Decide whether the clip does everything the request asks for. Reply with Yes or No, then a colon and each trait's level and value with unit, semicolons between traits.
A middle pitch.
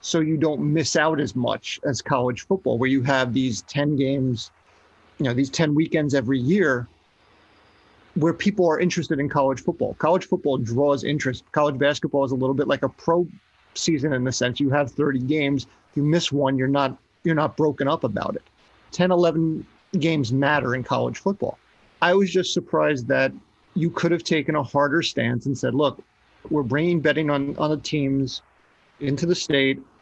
Yes: medium, 145 Hz